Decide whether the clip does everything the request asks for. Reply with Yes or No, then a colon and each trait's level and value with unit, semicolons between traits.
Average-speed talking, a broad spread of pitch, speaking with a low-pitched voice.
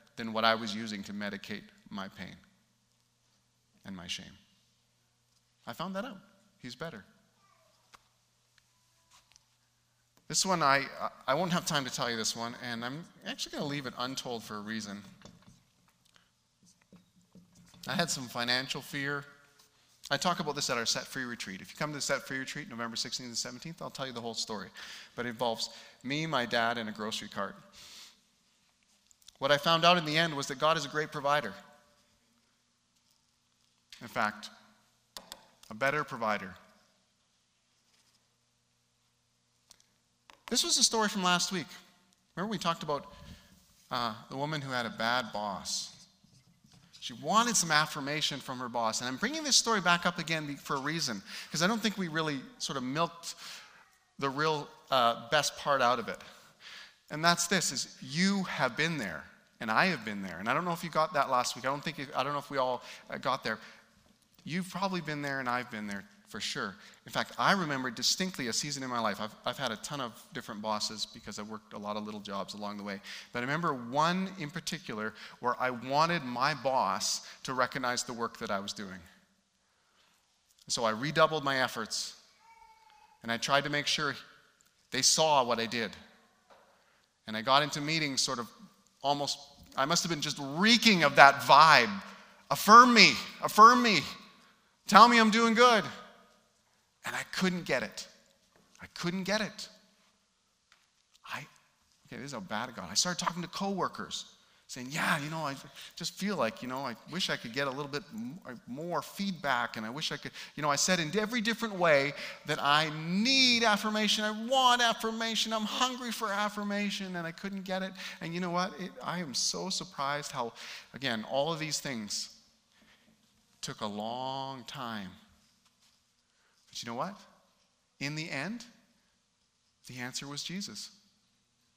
No: average, 180 wpm; wide, 7.5 semitones; medium, 145 Hz